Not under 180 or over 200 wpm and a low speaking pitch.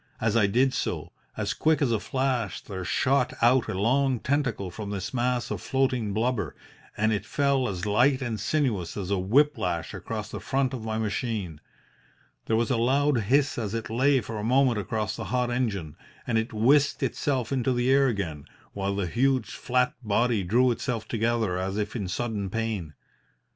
Yes: average, 190 wpm; low, 115 Hz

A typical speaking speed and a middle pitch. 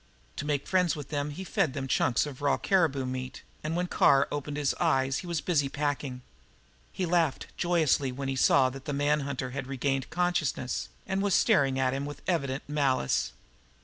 Yes: average, 190 wpm; medium, 145 Hz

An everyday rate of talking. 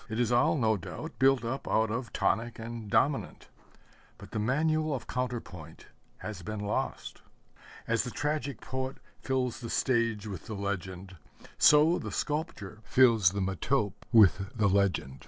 Yes: average, 155 wpm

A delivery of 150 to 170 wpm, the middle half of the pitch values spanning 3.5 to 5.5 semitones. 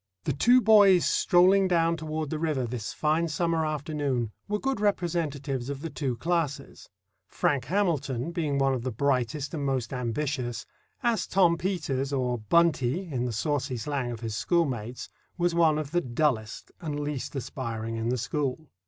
Yes: average, 160 wpm; average, 4.9 semitones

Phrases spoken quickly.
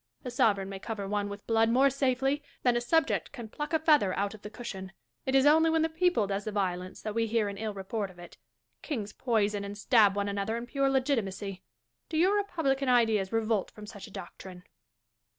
Yes: fast, 215 wpm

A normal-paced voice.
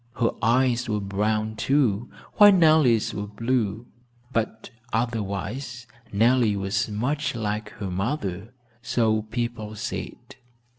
No: slow, 110 wpm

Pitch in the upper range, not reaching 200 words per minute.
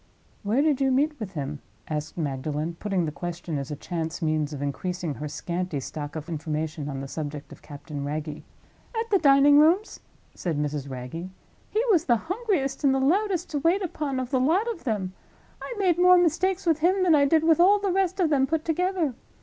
No: very high, 255 Hz; fast, 205 wpm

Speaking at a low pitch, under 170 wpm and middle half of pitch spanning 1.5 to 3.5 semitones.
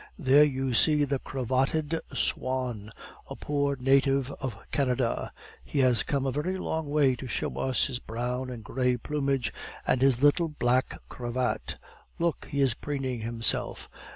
Yes: low, 130 Hz; average, 155 wpm; narrow, 2.4 semitones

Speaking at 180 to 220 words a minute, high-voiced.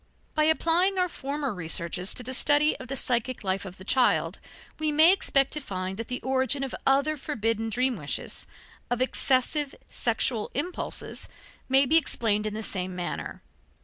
No: average, 170 wpm; very high, 255 Hz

